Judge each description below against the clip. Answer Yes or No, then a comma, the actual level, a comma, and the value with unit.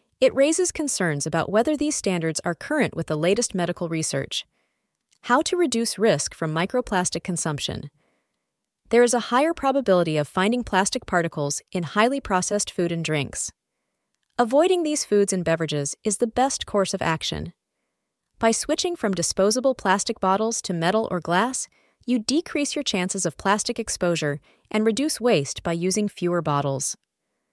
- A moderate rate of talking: Yes, average, 155 wpm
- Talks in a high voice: Yes, high, 200 Hz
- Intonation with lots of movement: Yes, wide, 6.4 semitones